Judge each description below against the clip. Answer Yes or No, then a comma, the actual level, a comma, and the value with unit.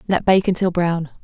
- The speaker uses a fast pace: No, average, 195 wpm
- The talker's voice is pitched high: No, medium, 180 Hz